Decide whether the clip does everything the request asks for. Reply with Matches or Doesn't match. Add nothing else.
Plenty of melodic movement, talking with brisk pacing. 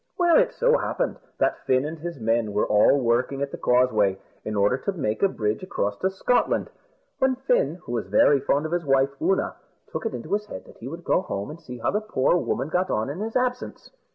Matches